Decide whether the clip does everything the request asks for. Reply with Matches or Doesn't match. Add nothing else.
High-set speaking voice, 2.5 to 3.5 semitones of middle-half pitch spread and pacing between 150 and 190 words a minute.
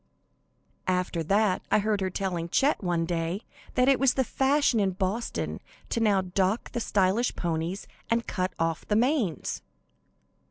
Doesn't match